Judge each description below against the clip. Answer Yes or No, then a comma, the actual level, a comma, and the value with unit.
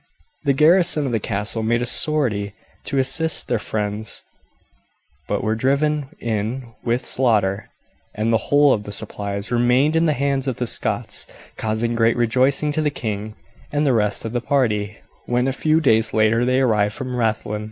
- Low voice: Yes, low, 120 Hz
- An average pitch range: Yes, average, 4.1 semitones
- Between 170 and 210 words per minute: Yes, average, 175 wpm